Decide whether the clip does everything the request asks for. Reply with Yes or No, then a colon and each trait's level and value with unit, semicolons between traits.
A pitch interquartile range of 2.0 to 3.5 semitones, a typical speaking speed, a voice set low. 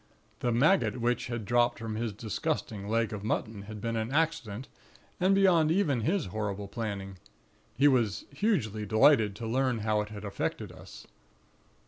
No: average, 4.2 semitones; average, 160 wpm; low, 115 Hz